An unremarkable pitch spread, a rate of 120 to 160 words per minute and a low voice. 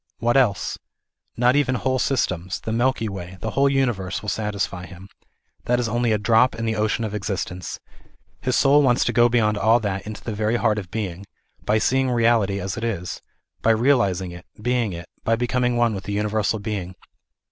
No: average, 3.6 semitones; average, 195 wpm; low, 110 Hz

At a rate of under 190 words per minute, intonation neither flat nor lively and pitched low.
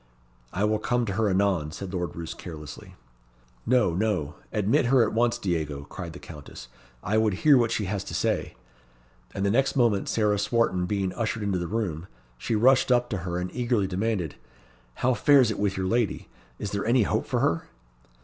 No: average, 195 wpm; average, 4.2 semitones; low, 105 Hz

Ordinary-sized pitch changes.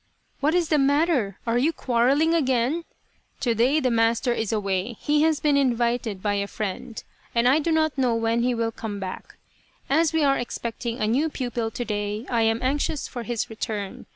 Yes: average, 4.2 semitones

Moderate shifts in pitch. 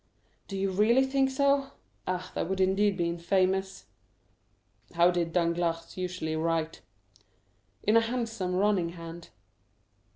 Yes: average, 3.6 semitones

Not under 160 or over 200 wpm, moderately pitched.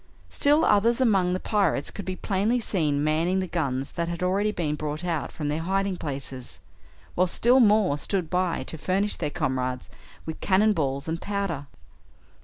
Yes: average, 175 wpm; medium, 180 Hz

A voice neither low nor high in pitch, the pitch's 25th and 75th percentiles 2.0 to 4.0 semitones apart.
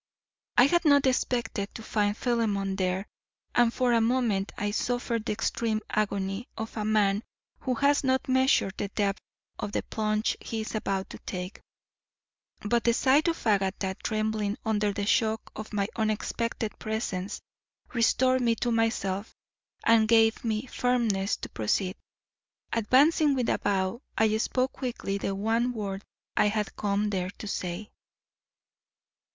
No: high, 220 Hz; average, 3.0 semitones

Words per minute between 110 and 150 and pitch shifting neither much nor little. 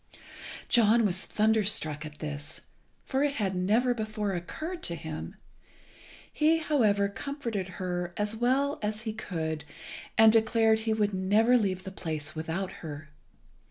Yes: average, 140 wpm; average, 4.4 semitones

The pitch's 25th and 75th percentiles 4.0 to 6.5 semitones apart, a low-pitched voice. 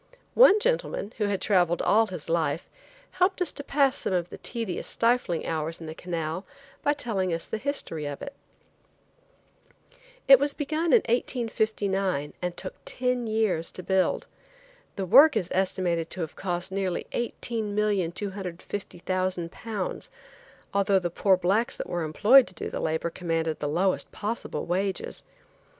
No: average, 4.9 semitones; high, 190 Hz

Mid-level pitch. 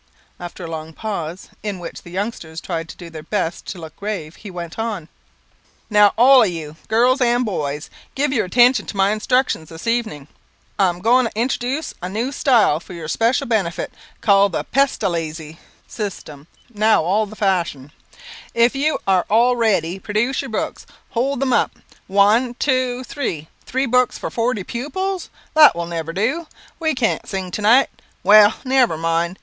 No: high, 210 Hz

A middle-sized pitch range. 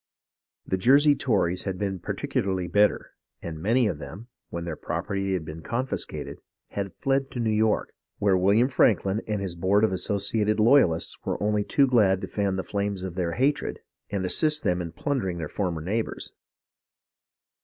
Yes: average, 3.5 semitones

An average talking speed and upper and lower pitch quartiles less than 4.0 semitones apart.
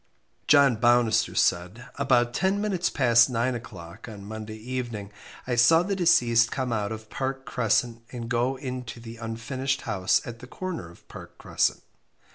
Yes: average, 160 wpm; average, 2.9 semitones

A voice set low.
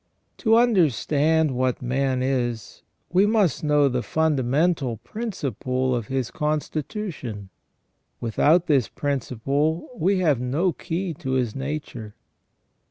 No: medium, 145 Hz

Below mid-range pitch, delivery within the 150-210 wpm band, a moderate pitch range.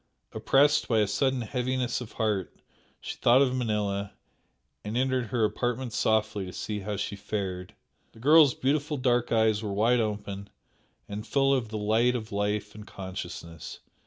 Yes: low, 110 Hz; average, 160 wpm; average, 3.5 semitones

